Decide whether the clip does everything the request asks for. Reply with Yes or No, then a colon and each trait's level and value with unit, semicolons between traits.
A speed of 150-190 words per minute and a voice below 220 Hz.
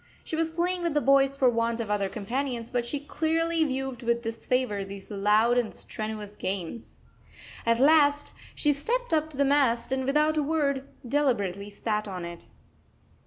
No: average, 170 wpm; very high, 255 Hz